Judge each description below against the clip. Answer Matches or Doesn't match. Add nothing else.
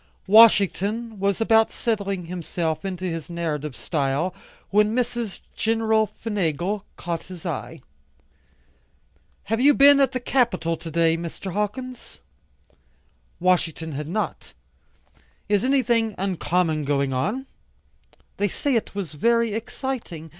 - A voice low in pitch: Doesn't match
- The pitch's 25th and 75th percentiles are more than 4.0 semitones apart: Matches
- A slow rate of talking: Matches